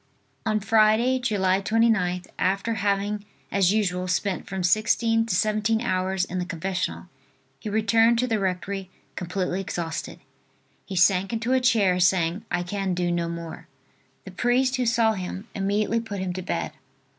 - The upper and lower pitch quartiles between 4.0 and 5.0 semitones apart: No, average, 3.5 semitones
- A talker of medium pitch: No, high, 195 Hz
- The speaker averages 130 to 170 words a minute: Yes, average, 155 wpm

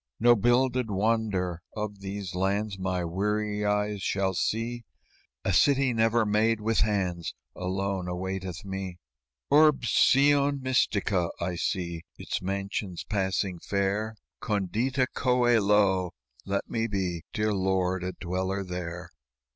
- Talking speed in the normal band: No, slow, 120 wpm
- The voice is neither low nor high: No, low, 100 Hz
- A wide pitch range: No, average, 3.1 semitones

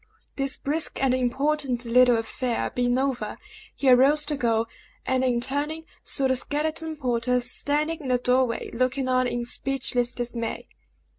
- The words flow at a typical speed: Yes, average, 155 wpm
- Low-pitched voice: No, very high, 255 Hz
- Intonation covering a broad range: No, narrow, 2.6 semitones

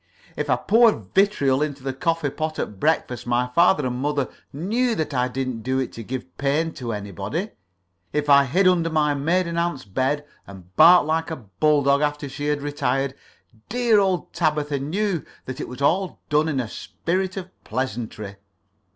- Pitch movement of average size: Yes, average, 4.5 semitones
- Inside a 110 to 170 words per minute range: No, average, 180 wpm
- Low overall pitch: No, medium, 145 Hz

